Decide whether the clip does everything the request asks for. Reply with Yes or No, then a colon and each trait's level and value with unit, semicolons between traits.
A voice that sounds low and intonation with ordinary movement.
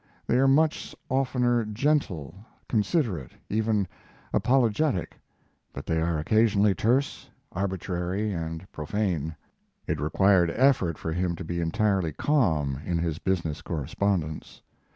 No: very low, 95 Hz; wide, 5.7 semitones